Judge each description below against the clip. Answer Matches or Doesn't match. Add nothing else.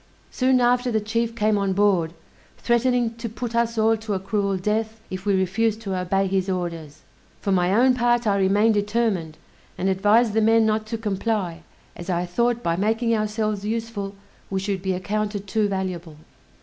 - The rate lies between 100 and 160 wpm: Doesn't match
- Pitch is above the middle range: Matches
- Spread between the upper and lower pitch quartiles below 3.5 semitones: Matches